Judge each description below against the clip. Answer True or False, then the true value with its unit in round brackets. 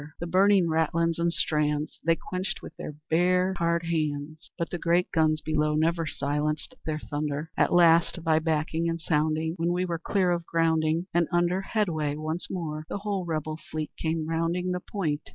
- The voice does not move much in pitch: True (2.0 semitones)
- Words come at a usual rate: True (180 wpm)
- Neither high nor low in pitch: True (165 Hz)